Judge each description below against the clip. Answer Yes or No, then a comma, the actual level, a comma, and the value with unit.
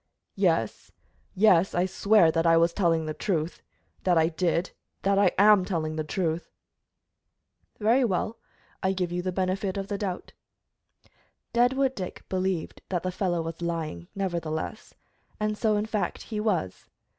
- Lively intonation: No, average, 3.5 semitones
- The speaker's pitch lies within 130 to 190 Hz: Yes, medium, 185 Hz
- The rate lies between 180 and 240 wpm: No, average, 155 wpm